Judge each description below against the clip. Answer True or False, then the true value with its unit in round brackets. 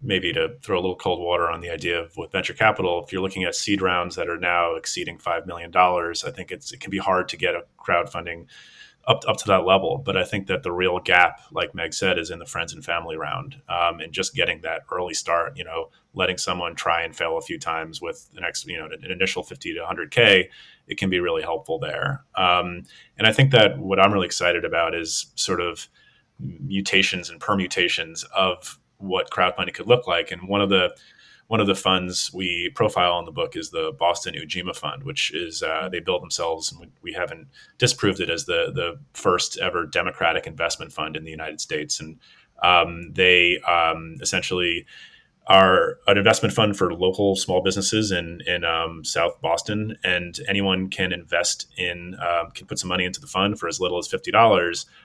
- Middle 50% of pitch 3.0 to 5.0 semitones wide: False (2.4 semitones)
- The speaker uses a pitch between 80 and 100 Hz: True (90 Hz)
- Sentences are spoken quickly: True (210 wpm)